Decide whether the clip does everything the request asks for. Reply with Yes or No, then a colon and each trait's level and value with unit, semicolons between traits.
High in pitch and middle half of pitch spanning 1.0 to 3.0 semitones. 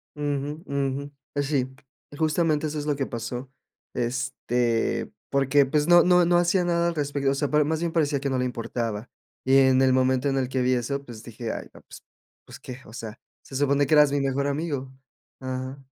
No: medium, 140 Hz; narrow, 2.4 semitones